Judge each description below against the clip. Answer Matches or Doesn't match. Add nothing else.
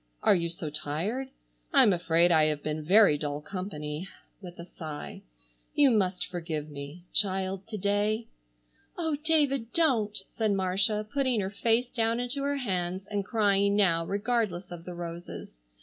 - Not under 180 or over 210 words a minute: Doesn't match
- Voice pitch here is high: Matches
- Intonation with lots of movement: Doesn't match